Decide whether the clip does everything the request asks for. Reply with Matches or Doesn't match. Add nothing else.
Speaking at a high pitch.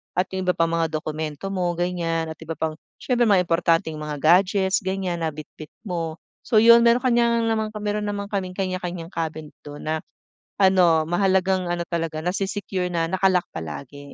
Doesn't match